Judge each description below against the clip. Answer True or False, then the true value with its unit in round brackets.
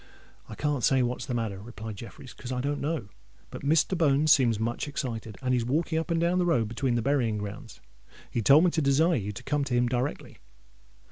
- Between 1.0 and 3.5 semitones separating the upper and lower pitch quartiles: False (4.3 semitones)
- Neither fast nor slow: False (215 wpm)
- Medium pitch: False (130 Hz)